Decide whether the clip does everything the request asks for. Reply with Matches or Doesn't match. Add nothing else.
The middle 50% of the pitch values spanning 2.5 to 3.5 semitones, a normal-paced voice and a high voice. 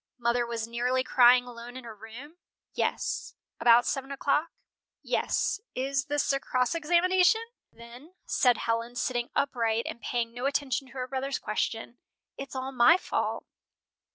Matches